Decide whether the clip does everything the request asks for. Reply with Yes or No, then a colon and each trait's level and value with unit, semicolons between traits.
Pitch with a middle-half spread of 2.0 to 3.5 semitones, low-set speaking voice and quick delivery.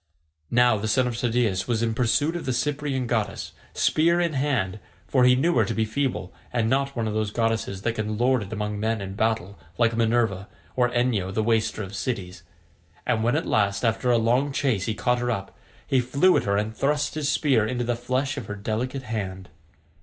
Yes: average, 3.2 semitones; low, 115 Hz; fast, 215 wpm